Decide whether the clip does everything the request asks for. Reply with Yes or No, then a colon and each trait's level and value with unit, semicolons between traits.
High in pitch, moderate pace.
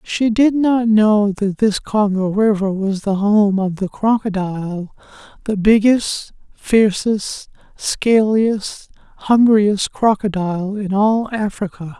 No: high, 205 Hz; slow, 115 wpm